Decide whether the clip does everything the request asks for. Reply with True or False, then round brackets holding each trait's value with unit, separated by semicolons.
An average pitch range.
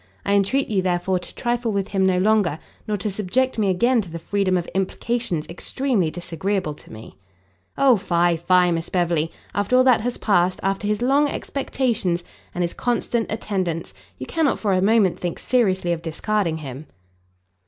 True (4.5 semitones)